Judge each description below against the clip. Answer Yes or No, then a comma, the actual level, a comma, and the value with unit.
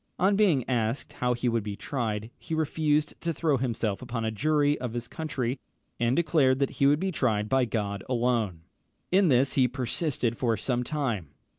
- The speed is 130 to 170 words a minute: No, average, 185 wpm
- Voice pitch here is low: Yes, low, 125 Hz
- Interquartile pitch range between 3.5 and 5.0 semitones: Yes, average, 4.3 semitones